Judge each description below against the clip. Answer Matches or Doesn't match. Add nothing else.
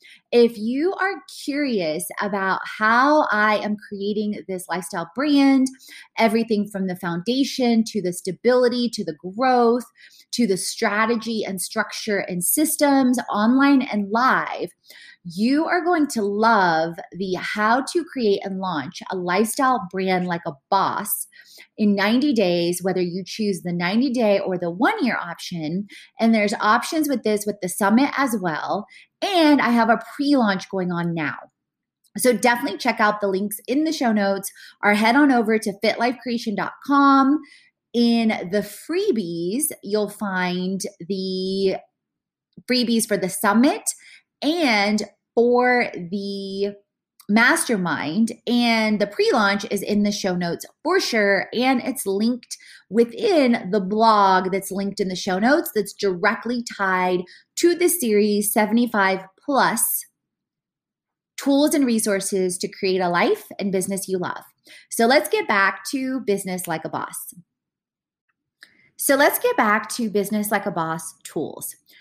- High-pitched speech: Matches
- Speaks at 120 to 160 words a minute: Matches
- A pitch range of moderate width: Matches